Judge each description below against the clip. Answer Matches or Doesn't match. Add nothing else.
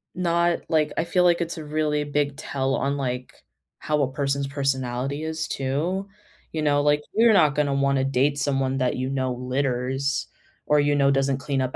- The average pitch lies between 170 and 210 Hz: Doesn't match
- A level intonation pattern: Matches